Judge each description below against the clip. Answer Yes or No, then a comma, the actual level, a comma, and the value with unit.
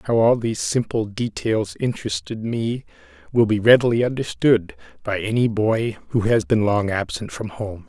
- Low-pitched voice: Yes, low, 110 Hz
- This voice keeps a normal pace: Yes, average, 160 wpm